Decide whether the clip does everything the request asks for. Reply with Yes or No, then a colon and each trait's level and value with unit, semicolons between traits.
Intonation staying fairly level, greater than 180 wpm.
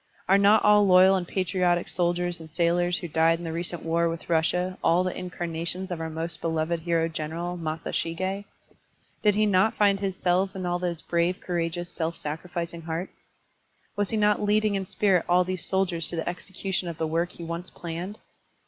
Yes: narrow, 2.2 semitones; average, 195 wpm